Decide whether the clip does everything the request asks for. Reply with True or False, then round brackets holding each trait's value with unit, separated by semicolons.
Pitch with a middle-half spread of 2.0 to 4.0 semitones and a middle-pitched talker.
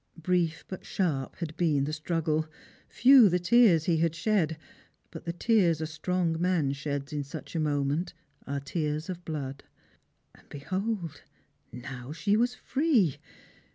True (3.5 semitones; 165 Hz)